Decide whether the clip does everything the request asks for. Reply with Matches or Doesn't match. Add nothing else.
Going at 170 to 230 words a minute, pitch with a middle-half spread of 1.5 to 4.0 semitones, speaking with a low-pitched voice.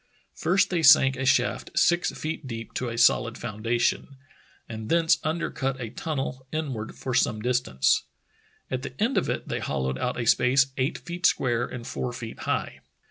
Doesn't match